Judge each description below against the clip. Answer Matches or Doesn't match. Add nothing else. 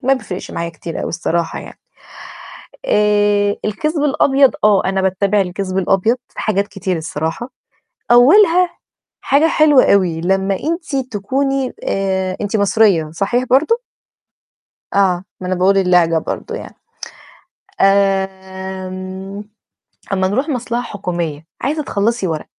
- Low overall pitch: Doesn't match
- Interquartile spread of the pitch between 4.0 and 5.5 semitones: Matches